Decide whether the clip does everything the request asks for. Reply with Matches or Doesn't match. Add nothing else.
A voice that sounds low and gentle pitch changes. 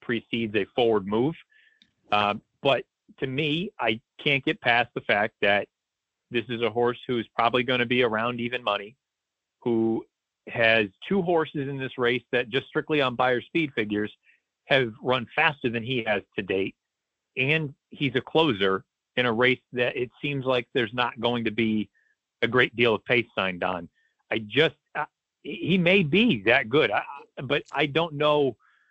Doesn't match